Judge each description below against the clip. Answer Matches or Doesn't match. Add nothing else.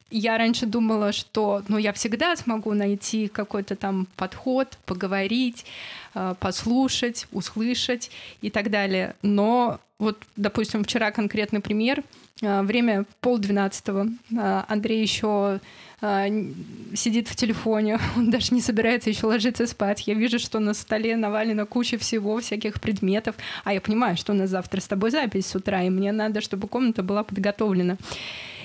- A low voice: Doesn't match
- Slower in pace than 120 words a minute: Doesn't match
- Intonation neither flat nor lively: Doesn't match